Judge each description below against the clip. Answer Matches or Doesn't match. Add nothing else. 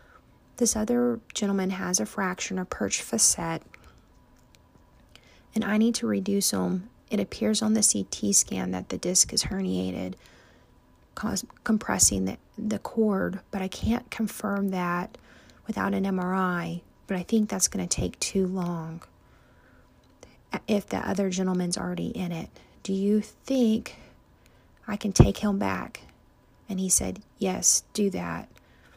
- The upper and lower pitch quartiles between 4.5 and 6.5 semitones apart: Doesn't match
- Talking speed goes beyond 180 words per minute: Doesn't match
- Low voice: Doesn't match